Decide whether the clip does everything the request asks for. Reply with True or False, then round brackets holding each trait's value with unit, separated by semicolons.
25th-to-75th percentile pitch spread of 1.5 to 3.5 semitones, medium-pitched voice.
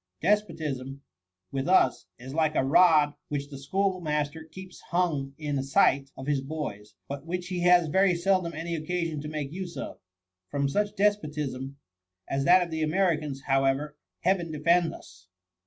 False (4.2 semitones; 155 Hz)